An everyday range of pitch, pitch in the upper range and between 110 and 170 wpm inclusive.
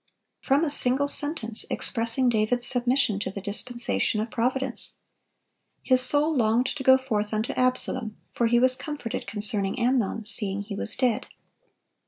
Yes: average, 3.3 semitones; high, 240 Hz; average, 150 wpm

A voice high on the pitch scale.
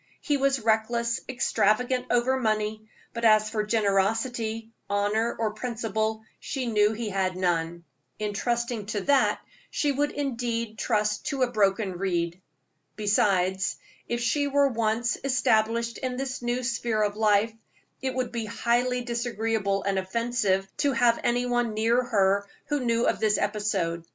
Yes: high, 225 Hz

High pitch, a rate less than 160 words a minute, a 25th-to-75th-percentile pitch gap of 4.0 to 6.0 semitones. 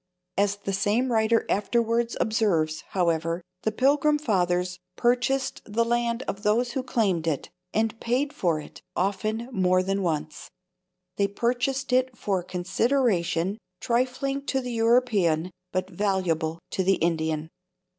Yes: high, 205 Hz; slow, 135 wpm; average, 5.0 semitones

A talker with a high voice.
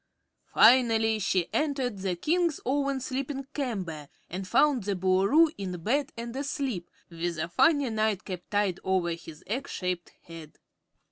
Yes: high, 215 Hz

